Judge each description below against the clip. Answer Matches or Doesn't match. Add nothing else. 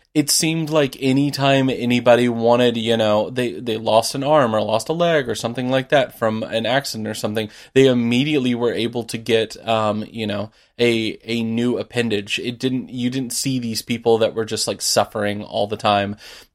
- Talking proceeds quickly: Doesn't match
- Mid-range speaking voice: Doesn't match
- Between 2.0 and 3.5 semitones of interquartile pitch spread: Matches